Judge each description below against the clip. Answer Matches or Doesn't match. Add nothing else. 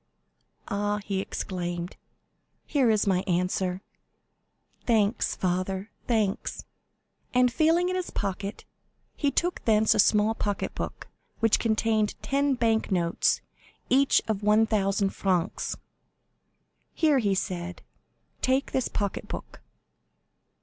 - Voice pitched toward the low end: Doesn't match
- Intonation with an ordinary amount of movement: Matches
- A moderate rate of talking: Doesn't match